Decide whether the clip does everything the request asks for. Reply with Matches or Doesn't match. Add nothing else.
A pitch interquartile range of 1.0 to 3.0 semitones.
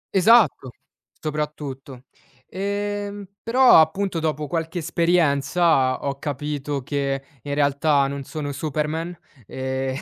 Doesn't match